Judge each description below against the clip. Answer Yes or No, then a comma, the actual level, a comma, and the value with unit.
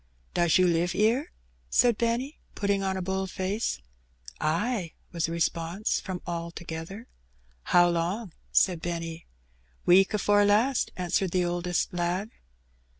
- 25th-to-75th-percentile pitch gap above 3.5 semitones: No, average, 3.2 semitones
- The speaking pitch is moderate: Yes, medium, 180 Hz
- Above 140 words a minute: No, slow, 135 wpm